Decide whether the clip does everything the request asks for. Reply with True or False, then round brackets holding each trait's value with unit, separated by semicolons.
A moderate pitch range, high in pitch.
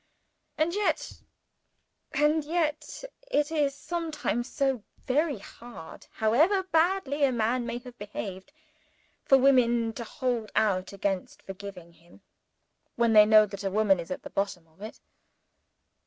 False (6.6 semitones; 240 Hz)